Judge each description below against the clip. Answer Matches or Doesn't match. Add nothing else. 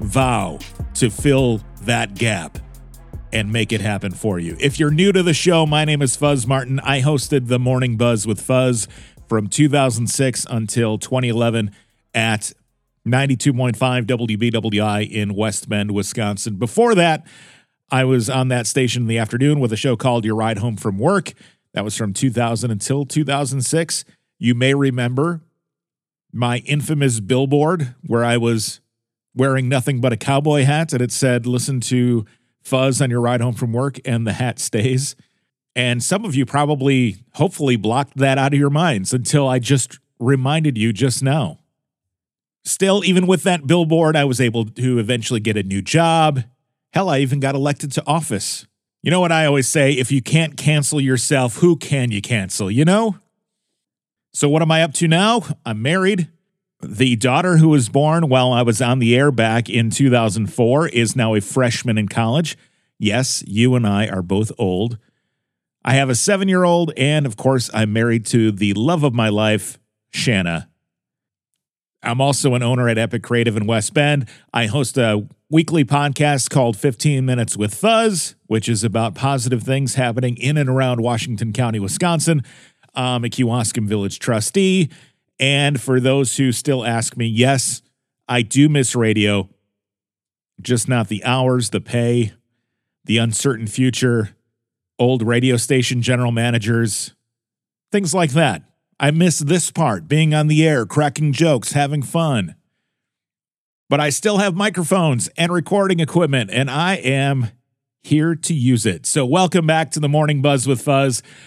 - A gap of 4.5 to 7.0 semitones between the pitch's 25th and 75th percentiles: Doesn't match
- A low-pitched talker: Matches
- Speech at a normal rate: Matches